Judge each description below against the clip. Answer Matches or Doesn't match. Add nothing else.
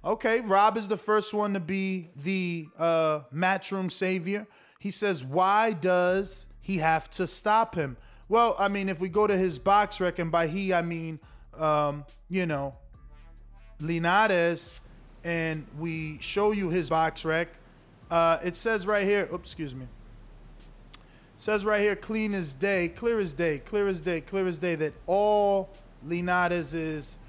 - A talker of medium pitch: Matches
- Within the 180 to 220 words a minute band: Doesn't match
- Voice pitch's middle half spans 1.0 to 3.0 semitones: Doesn't match